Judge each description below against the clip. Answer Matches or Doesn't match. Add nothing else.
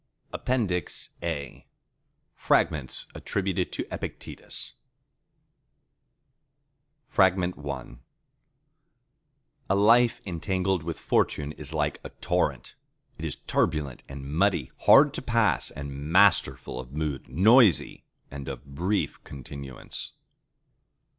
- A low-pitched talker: Matches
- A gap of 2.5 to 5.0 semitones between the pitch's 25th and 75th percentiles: Doesn't match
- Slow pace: Matches